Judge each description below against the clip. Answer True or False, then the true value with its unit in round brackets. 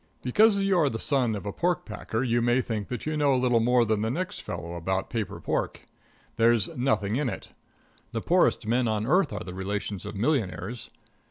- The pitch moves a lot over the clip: False (4.6 semitones)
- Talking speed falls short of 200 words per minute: False (205 wpm)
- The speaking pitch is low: True (120 Hz)